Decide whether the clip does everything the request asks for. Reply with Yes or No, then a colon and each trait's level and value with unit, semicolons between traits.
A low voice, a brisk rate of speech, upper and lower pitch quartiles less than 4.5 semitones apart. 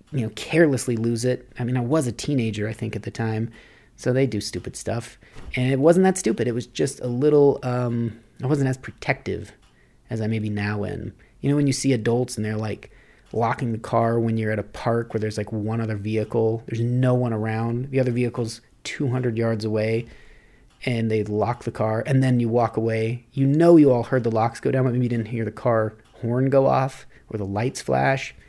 Yes: low, 115 Hz; fast, 225 wpm; narrow, 2.5 semitones